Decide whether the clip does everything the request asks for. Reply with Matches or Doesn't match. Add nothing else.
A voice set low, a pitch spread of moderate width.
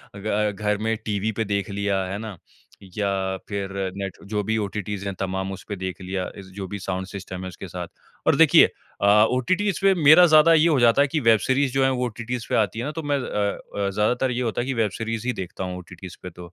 Matches